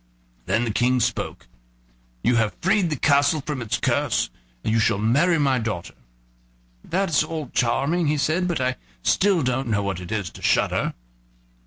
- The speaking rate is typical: Yes, average, 170 wpm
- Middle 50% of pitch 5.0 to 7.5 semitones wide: Yes, average, 5.3 semitones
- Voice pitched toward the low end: Yes, low, 130 Hz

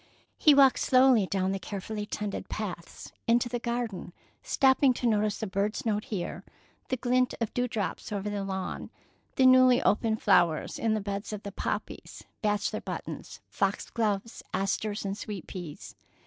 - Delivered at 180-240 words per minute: No, average, 155 wpm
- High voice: Yes, high, 210 Hz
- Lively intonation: No, average, 3.6 semitones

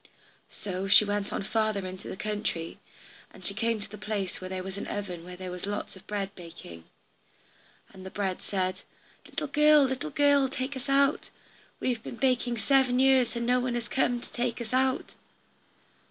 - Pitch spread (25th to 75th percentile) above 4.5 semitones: Yes, average, 5.2 semitones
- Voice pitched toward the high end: Yes, high, 215 Hz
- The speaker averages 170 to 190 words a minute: No, fast, 205 wpm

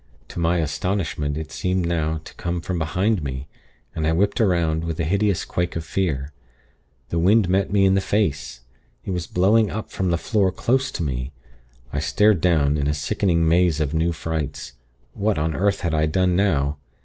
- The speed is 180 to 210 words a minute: Yes, average, 195 wpm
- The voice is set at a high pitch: No, very low, 85 Hz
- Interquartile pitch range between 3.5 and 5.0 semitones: Yes, average, 3.8 semitones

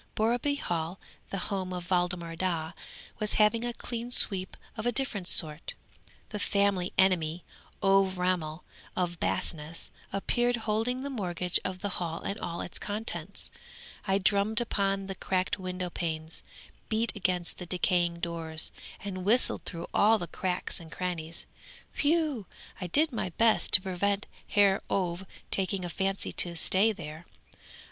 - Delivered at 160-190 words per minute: No, average, 150 wpm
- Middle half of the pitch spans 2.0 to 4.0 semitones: Yes, average, 3.3 semitones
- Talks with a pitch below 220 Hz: Yes, medium, 185 Hz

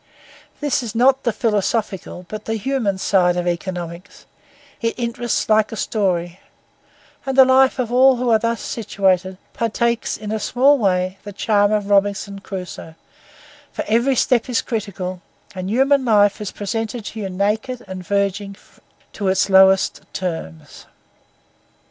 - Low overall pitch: No, high, 210 Hz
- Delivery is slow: No, average, 145 wpm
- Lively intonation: No, average, 3.7 semitones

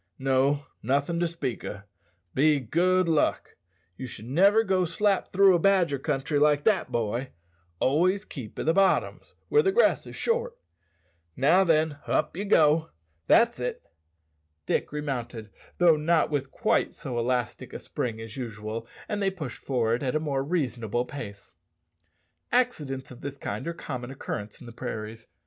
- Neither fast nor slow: Yes, average, 165 wpm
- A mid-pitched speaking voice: Yes, medium, 145 Hz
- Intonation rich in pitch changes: Yes, wide, 6.3 semitones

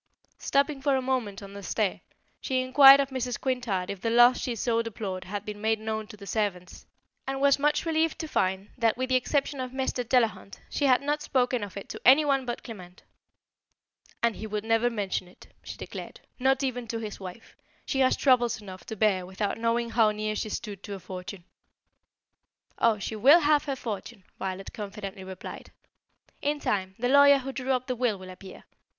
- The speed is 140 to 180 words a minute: No, average, 200 wpm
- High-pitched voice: Yes, high, 230 Hz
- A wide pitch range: No, average, 4.6 semitones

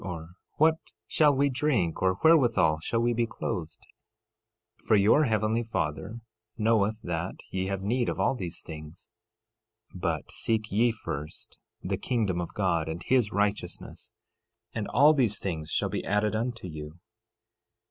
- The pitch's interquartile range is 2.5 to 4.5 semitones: No, wide, 5.4 semitones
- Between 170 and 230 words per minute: No, average, 155 wpm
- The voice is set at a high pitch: No, low, 105 Hz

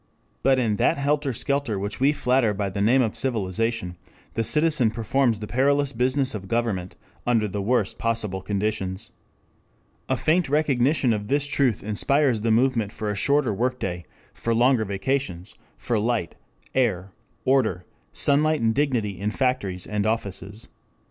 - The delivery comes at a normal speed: Yes, average, 155 wpm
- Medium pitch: No, low, 115 Hz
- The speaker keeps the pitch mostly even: No, average, 4.5 semitones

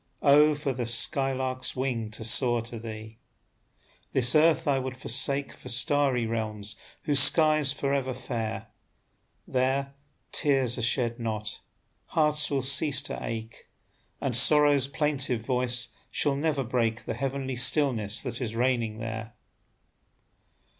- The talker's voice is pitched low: Yes, low, 130 Hz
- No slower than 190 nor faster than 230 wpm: No, slow, 135 wpm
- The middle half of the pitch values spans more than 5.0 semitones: No, average, 3.3 semitones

